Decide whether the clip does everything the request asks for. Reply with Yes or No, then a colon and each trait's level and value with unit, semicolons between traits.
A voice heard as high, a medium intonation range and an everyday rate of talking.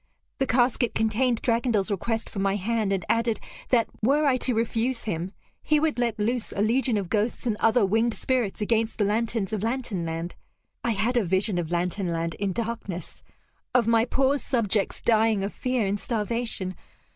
Yes: high, 225 Hz; average, 3.3 semitones; average, 180 wpm